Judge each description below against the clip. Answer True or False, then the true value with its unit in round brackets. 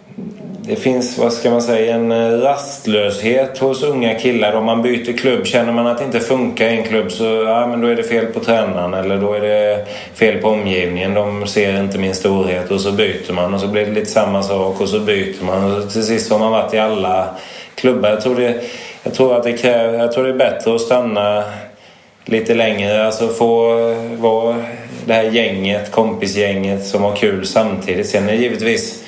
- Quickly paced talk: True (210 wpm)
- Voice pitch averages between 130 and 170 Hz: False (115 Hz)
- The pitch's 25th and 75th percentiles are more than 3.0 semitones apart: False (2.5 semitones)